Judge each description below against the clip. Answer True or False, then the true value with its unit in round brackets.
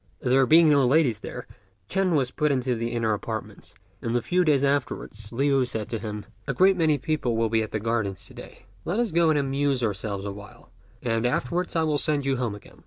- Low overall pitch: True (130 Hz)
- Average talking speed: False (220 wpm)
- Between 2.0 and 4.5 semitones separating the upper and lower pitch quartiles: False (5.2 semitones)